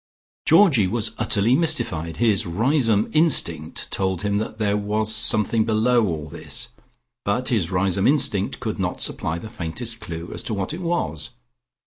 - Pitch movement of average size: Yes, average, 4.2 semitones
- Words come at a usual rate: Yes, average, 155 wpm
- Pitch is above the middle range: No, low, 105 Hz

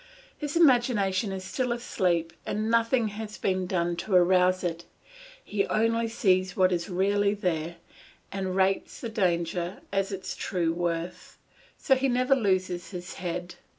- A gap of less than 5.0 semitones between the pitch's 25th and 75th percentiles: Yes, average, 3.6 semitones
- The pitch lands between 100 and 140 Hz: No, high, 190 Hz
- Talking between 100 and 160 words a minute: Yes, average, 150 wpm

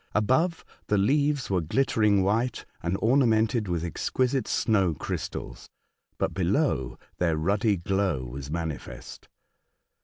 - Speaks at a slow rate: Yes, slow, 115 wpm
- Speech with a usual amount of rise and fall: No, wide, 6.1 semitones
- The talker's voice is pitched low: Yes, low, 100 Hz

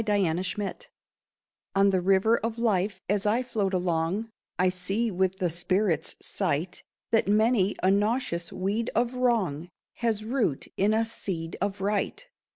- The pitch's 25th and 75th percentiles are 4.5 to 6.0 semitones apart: No, average, 3.4 semitones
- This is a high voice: Yes, high, 200 Hz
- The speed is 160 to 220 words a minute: No, average, 145 wpm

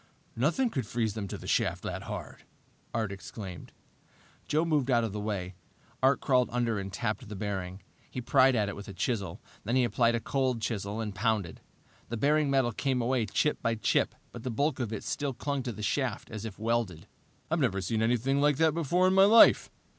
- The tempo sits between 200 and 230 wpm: Yes, fast, 205 wpm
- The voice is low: Yes, low, 115 Hz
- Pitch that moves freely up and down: No, average, 4.3 semitones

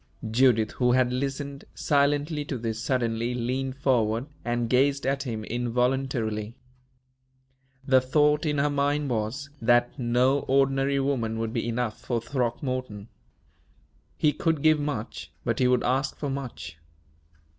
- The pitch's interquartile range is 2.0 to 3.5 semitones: Yes, average, 3.0 semitones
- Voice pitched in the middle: No, low, 130 Hz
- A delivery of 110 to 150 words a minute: Yes, slow, 135 wpm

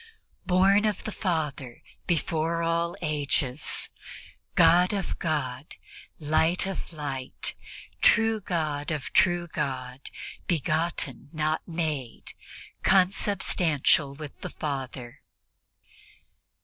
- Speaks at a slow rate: Yes, slow, 90 wpm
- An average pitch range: Yes, average, 3.6 semitones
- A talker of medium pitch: Yes, medium, 155 Hz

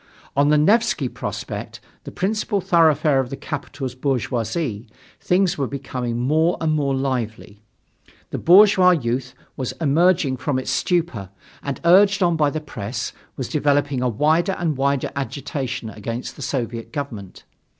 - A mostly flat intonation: No, average, 4.7 semitones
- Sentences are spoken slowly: No, average, 145 wpm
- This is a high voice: No, medium, 140 Hz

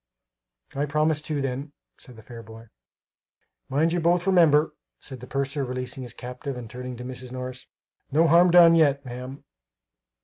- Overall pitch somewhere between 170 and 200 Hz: No, low, 135 Hz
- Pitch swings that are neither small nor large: Yes, average, 3.5 semitones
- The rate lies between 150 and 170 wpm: Yes, average, 165 wpm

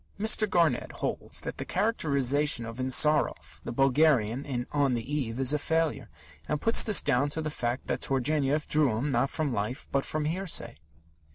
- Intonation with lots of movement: No, average, 3.6 semitones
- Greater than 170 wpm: Yes, average, 180 wpm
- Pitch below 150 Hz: Yes, medium, 140 Hz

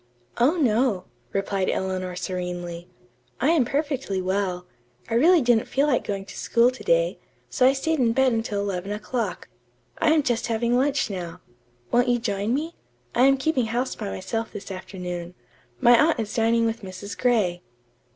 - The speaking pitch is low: No, high, 230 Hz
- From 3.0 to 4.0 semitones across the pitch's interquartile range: No, average, 5.3 semitones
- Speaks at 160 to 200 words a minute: Yes, average, 170 wpm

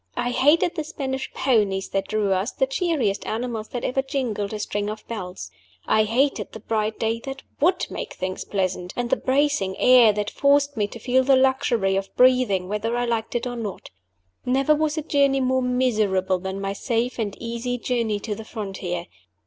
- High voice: Yes, high, 235 Hz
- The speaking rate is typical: Yes, average, 190 wpm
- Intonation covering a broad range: No, average, 4.4 semitones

